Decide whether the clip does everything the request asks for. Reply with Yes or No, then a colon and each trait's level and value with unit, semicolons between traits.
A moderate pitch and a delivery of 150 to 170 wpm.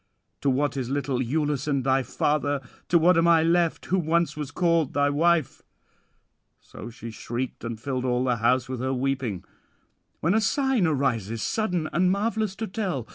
No: medium, 145 Hz; average, 180 wpm